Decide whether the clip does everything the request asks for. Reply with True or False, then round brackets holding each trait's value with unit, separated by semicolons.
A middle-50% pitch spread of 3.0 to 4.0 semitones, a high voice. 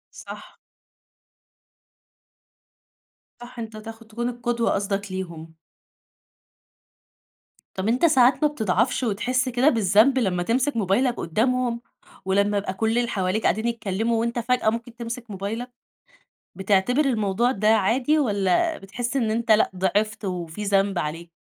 True (3.7 semitones; 225 Hz)